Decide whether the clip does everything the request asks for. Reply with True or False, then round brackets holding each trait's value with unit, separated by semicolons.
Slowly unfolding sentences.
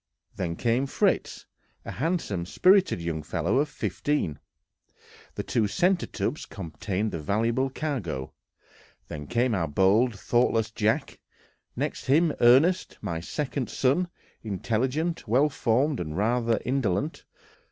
True (120 wpm)